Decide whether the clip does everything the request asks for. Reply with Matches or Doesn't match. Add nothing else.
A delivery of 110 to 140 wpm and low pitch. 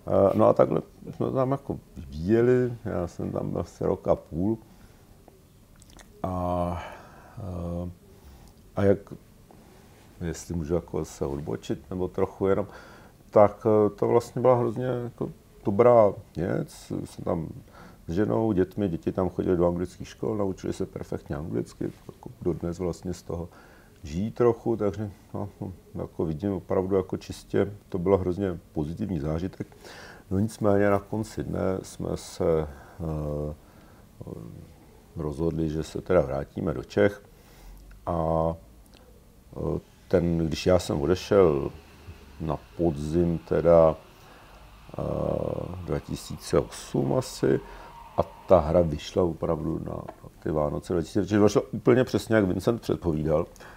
Matches